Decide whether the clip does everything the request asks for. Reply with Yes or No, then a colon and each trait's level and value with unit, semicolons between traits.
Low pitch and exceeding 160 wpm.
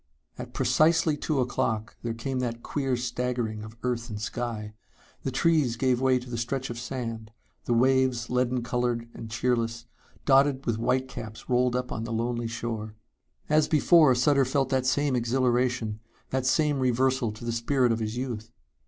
Yes: low, 125 Hz; average, 170 wpm